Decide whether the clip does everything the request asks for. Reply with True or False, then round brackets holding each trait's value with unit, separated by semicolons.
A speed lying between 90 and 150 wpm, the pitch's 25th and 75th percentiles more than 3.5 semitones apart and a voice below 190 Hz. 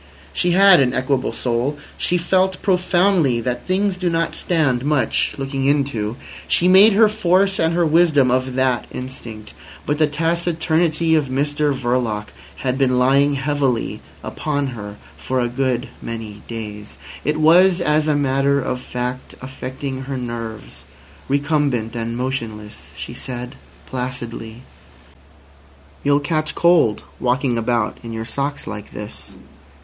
True (140 wpm; 4.4 semitones; 135 Hz)